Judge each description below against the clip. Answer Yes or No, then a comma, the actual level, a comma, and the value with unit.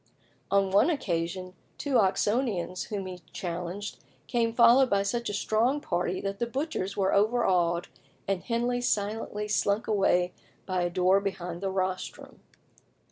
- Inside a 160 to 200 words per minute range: No, average, 140 wpm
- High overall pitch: Yes, high, 200 Hz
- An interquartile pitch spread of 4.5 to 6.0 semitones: No, average, 4.1 semitones